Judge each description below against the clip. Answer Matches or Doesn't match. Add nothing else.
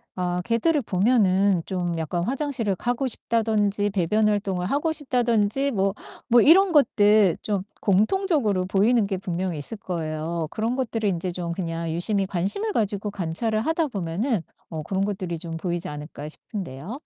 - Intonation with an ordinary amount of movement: Matches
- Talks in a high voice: Matches